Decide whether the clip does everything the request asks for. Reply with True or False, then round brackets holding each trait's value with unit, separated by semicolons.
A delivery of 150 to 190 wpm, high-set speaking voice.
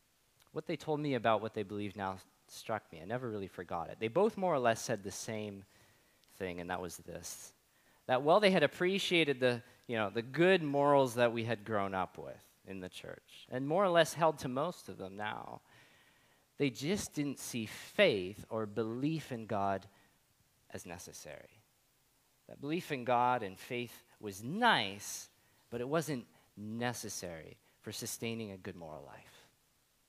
False (175 wpm; 115 Hz)